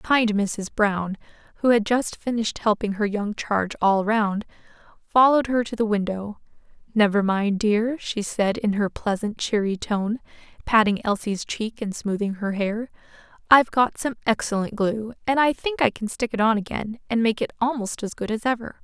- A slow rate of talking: No, average, 180 wpm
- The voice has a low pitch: No, high, 220 Hz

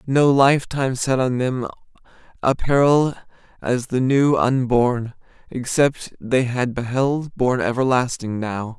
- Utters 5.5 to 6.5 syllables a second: No, 4.1 syllables/s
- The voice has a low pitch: Yes, low, 125 Hz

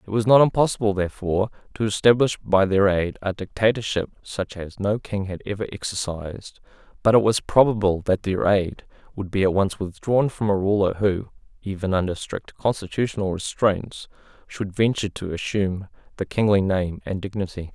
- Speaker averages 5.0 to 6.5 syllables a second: Yes, 5.3 syllables/s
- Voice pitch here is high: No, low, 100 Hz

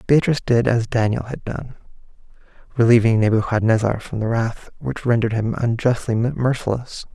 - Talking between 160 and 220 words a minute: No, slow, 135 wpm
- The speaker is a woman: No, male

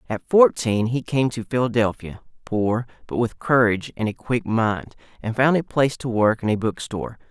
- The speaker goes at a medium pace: Yes, average, 190 wpm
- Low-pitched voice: Yes, low, 120 Hz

